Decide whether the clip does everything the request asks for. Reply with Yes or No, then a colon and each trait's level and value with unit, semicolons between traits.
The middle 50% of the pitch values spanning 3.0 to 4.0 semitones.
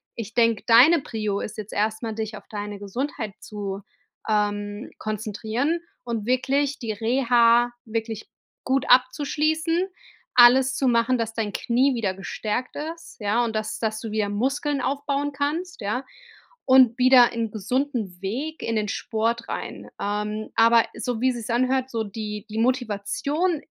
Yes: average, 3.5 semitones